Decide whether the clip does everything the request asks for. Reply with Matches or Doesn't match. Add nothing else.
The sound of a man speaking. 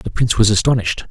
Matches